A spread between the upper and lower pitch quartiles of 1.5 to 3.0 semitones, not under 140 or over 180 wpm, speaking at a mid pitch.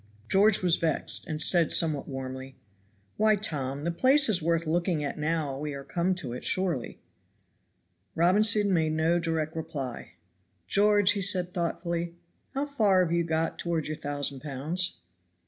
No: average, 3.6 semitones; average, 155 wpm; medium, 165 Hz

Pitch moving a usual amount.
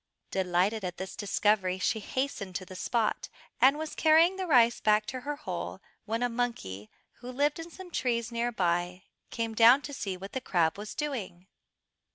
No: wide, 5.9 semitones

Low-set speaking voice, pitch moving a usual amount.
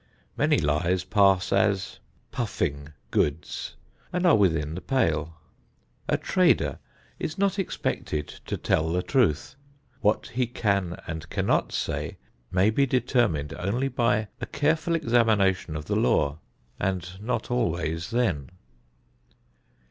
No: low, 100 Hz; wide, 7.0 semitones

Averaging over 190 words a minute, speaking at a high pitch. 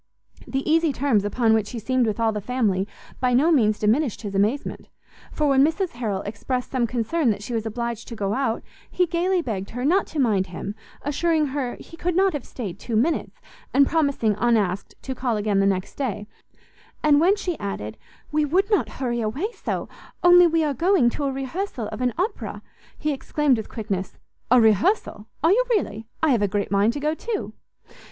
Yes: average, 200 wpm; very high, 250 Hz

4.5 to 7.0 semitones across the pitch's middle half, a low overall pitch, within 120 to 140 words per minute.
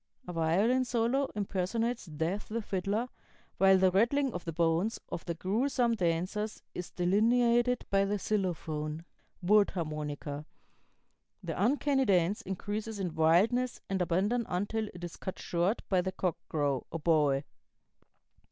No: average, 4.9 semitones; high, 190 Hz; slow, 135 wpm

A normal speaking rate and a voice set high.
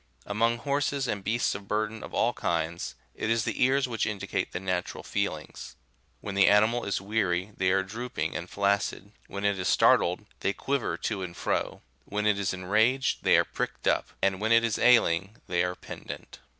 No: average, 195 wpm; low, 105 Hz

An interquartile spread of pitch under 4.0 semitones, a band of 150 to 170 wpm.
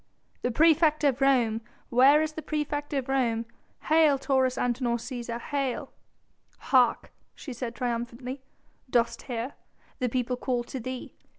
No: average, 2.9 semitones; slow, 135 wpm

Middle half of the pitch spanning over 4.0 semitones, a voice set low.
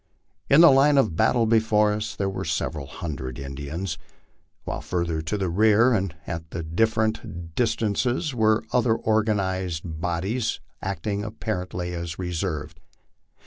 Yes: average, 4.8 semitones; very low, 95 Hz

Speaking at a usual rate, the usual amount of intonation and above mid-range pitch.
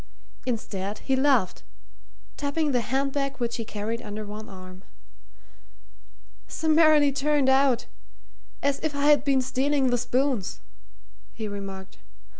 No: slow, 125 wpm; average, 4.8 semitones; very high, 260 Hz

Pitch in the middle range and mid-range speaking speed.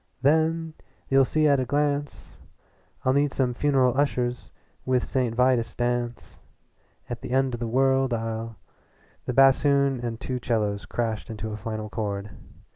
No: low, 125 Hz; average, 155 wpm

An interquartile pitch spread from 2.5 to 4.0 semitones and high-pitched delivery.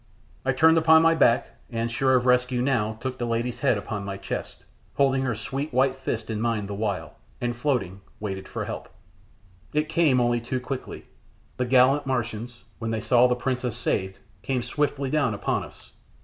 No: average, 2.9 semitones; low, 125 Hz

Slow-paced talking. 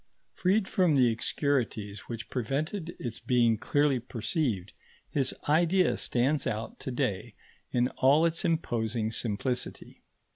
Yes: slow, 120 wpm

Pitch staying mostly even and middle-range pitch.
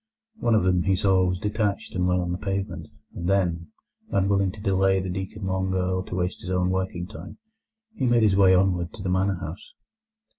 No: narrow, 1.5 semitones; very low, 95 Hz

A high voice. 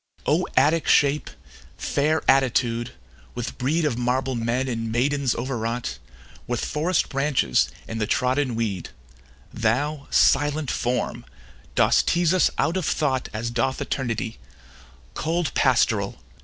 No: low, 130 Hz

